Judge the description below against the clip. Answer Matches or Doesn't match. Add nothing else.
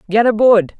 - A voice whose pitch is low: Doesn't match